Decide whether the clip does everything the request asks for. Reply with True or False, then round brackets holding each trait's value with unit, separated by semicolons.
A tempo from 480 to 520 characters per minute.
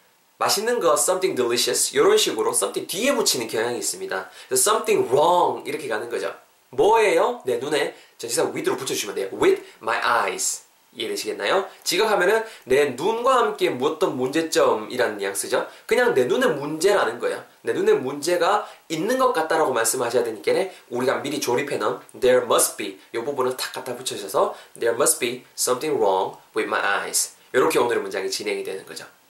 True (510 characters per minute)